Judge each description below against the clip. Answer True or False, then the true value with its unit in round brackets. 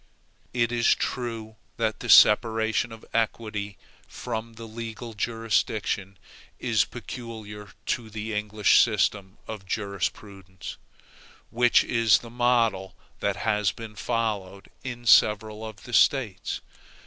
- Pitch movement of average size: False (1.9 semitones)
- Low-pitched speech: True (110 Hz)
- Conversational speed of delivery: False (120 wpm)